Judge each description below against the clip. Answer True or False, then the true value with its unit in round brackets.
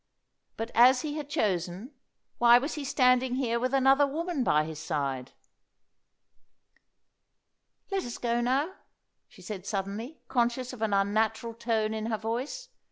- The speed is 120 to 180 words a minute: True (145 wpm)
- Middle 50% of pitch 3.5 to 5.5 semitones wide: True (3.8 semitones)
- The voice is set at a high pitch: True (235 Hz)